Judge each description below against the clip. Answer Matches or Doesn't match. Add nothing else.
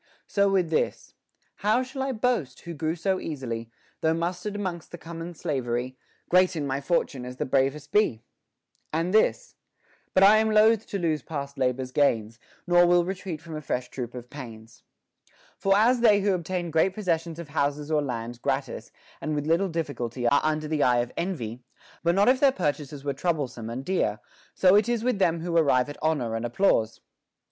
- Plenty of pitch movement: Matches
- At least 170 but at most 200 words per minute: Matches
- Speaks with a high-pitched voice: Doesn't match